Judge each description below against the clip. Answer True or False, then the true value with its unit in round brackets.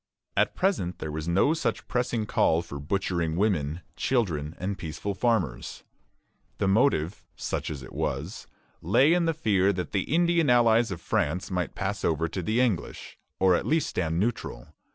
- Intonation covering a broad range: True (6.3 semitones)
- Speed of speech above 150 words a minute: True (170 wpm)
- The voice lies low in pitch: True (95 Hz)